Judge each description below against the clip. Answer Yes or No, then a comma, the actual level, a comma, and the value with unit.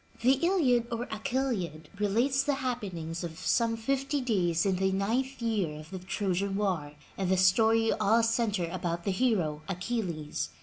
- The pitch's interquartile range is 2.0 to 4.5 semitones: No, average, 5.0 semitones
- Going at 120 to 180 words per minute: Yes, average, 165 wpm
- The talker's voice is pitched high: Yes, high, 205 Hz